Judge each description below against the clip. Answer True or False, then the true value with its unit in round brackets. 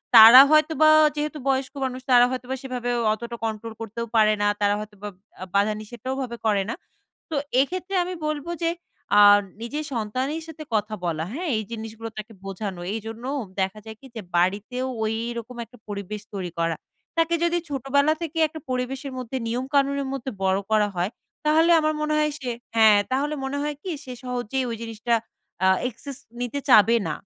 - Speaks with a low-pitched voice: False (245 Hz)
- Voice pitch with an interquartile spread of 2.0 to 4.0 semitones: False (4.6 semitones)